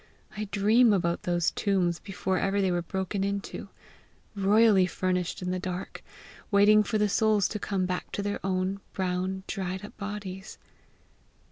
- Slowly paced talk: No, average, 155 wpm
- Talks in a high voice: Yes, high, 195 Hz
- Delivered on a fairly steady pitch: Yes, narrow, 1.9 semitones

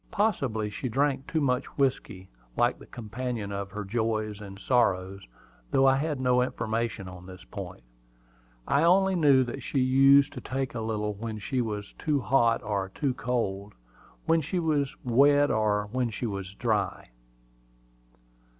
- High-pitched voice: No, low, 120 Hz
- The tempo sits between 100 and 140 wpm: No, average, 160 wpm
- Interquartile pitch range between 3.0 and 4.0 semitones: No, average, 4.6 semitones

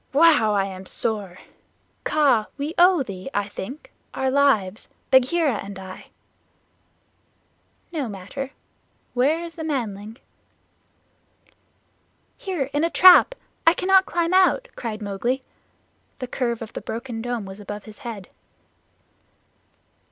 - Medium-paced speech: No, slow, 120 wpm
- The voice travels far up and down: Yes, wide, 6.9 semitones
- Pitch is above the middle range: Yes, high, 245 Hz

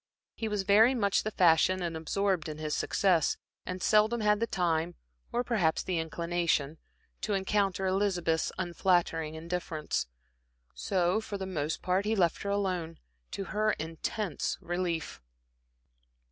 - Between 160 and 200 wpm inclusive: No, average, 140 wpm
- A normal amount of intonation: Yes, average, 3.6 semitones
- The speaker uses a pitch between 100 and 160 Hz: No, medium, 185 Hz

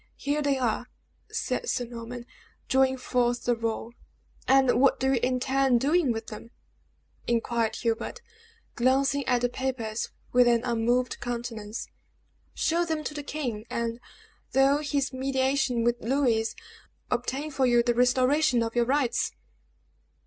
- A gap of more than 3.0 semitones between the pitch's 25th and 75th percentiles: No, narrow, 2.4 semitones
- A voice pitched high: Yes, very high, 250 Hz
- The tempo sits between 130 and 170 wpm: Yes, average, 140 wpm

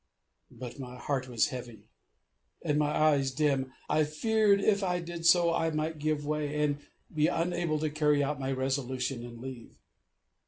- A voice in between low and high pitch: Yes, medium, 150 Hz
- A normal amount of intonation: Yes, average, 3.4 semitones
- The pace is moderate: Yes, average, 165 wpm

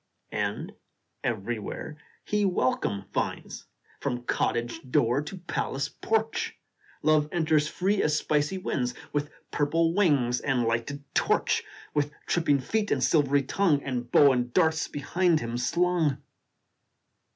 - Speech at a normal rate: No, slow, 125 wpm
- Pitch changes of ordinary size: Yes, average, 5.0 semitones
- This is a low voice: No, medium, 145 Hz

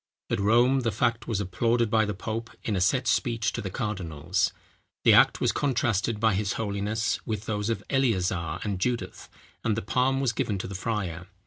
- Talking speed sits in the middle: Yes, average, 195 wpm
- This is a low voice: Yes, low, 110 Hz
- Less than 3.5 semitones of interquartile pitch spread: Yes, average, 2.8 semitones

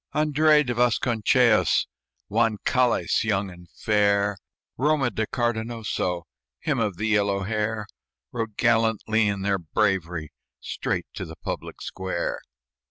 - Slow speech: Yes, slow, 120 wpm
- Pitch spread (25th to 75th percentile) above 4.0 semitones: No, average, 3.1 semitones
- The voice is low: Yes, low, 110 Hz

